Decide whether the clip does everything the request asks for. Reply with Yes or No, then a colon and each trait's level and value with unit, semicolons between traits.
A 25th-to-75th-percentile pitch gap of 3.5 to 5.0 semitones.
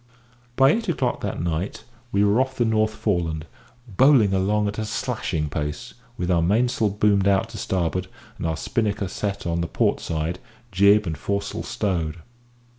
Yes: average, 4.1 semitones